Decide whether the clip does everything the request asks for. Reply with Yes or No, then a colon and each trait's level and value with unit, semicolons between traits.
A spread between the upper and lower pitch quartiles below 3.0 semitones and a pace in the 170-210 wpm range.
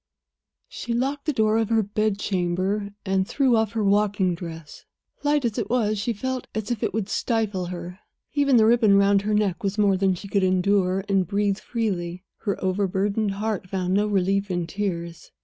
Yes: narrow, 2.6 semitones; average, 185 wpm